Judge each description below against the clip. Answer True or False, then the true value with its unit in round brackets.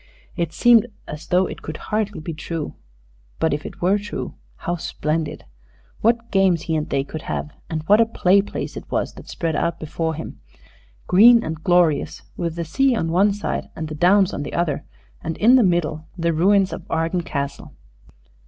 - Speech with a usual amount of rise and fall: True (4.1 semitones)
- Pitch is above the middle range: False (170 Hz)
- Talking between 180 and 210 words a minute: True (190 wpm)